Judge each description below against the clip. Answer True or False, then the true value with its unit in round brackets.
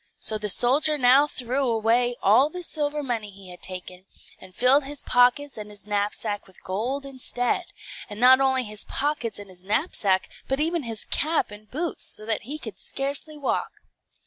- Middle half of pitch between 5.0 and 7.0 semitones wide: True (5.3 semitones)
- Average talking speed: True (180 wpm)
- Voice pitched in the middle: False (245 Hz)